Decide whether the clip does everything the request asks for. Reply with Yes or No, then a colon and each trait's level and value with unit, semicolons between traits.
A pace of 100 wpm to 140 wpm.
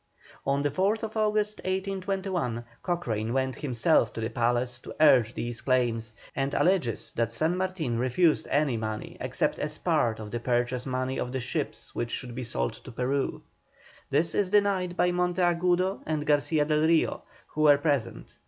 No: average, 165 wpm